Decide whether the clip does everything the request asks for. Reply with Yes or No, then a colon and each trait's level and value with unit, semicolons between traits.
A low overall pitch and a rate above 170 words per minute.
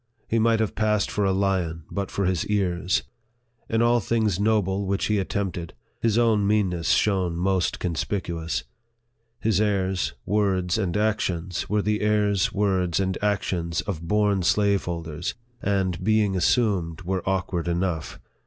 No: very low, 95 Hz; average, 145 wpm